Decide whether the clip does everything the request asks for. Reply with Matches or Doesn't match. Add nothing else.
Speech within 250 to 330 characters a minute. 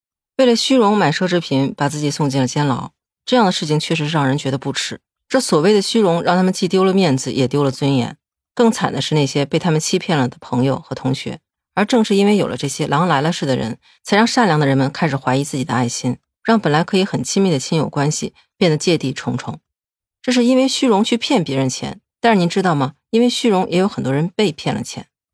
Doesn't match